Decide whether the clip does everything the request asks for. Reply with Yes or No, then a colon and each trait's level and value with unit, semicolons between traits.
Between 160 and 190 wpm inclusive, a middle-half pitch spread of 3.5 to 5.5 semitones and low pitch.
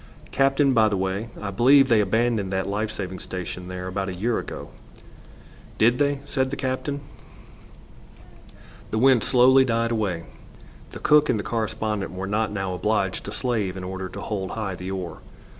Yes: average, 175 wpm; average, 4.3 semitones; low, 105 Hz